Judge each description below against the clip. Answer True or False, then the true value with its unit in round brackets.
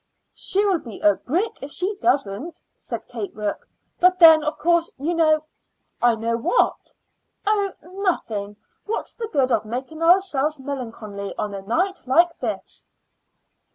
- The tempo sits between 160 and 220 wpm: False (150 wpm)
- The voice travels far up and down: True (7.8 semitones)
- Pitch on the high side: True (310 Hz)